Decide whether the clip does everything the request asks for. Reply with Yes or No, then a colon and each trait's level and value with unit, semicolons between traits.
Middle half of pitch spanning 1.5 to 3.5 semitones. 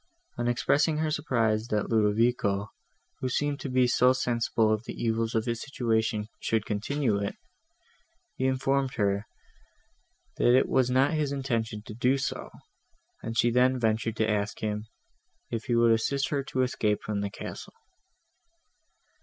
Yes: average, 3.2 semitones